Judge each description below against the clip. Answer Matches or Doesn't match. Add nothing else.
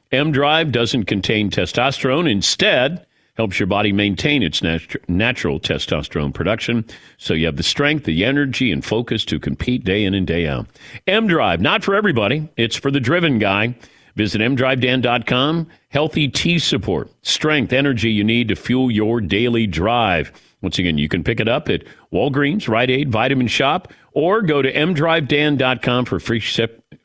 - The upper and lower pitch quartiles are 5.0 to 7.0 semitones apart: Matches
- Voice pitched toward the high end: Doesn't match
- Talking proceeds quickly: Doesn't match